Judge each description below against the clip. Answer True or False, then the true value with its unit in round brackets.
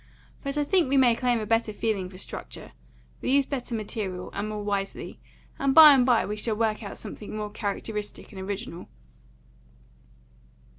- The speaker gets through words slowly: False (170 wpm)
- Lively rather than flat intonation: False (3.8 semitones)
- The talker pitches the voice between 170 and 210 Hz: False (220 Hz)